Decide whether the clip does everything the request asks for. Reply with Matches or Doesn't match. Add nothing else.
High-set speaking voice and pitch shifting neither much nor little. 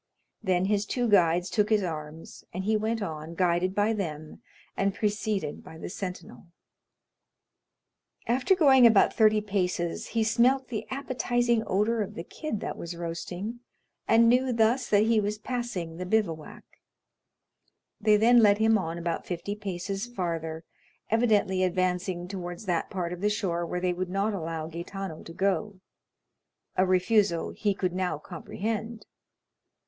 Matches